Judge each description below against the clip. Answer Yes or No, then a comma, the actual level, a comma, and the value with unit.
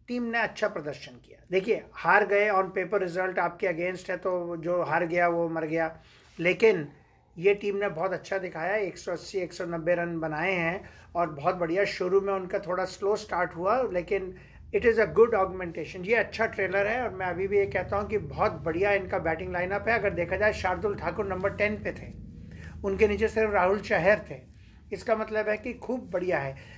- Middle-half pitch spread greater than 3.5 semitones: No, average, 2.9 semitones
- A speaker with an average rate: No, fast, 200 wpm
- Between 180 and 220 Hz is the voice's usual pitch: Yes, medium, 185 Hz